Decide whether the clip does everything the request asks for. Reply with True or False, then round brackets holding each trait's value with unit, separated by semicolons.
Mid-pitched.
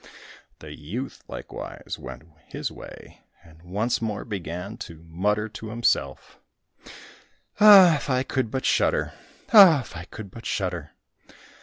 False (105 Hz)